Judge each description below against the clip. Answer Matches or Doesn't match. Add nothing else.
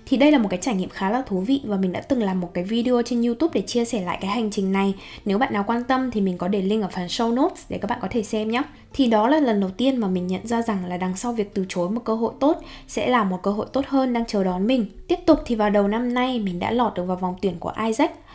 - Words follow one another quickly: Matches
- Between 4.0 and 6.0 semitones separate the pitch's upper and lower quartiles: Matches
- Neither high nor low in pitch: Doesn't match